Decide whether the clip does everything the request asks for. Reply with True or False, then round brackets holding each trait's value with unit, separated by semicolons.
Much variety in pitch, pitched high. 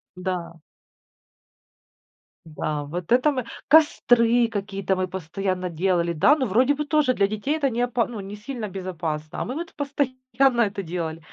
True (6.1 semitones; 210 Hz)